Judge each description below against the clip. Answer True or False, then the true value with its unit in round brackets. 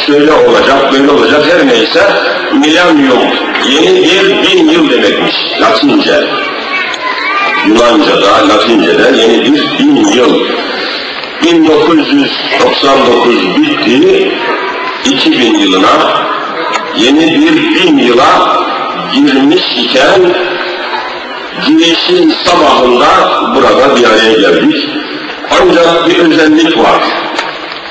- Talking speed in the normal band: False (85 wpm)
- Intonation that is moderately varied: True (3.6 semitones)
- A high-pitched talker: True (320 Hz)